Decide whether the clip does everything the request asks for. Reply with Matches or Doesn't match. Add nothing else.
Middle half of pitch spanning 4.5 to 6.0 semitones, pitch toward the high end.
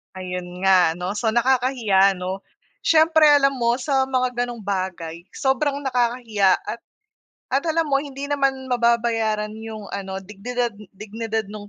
Matches